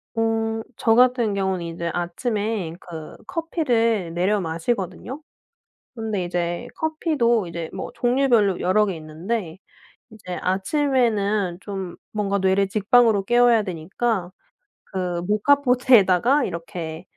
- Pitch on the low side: No, high, 205 Hz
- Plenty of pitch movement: No, average, 5.0 semitones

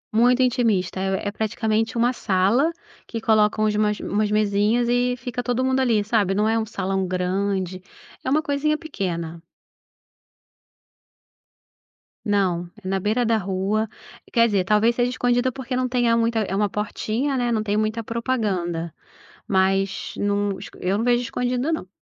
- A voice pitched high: Yes, high, 215 Hz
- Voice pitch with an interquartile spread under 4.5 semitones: Yes, average, 3.8 semitones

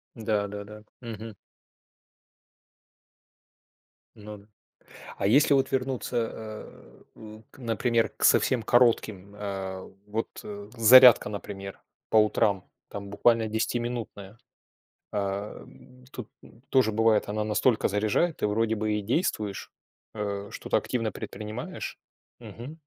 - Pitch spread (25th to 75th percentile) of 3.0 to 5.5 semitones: No, narrow, 2.5 semitones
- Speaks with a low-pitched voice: Yes, low, 110 Hz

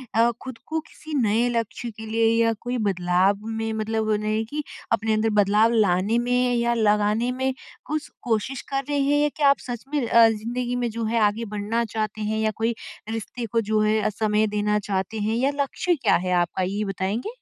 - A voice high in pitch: Yes, high, 225 Hz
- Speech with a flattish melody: Yes, narrow, 2.3 semitones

